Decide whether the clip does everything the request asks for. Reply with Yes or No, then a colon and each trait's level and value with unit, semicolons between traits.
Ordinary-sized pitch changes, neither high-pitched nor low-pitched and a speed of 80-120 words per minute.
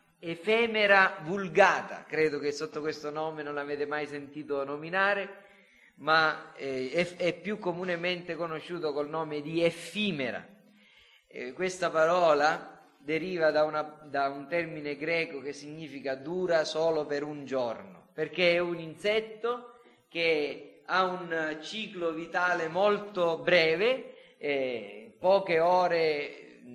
Yes: average, 3.5 semitones; medium, 165 Hz; slow, 115 wpm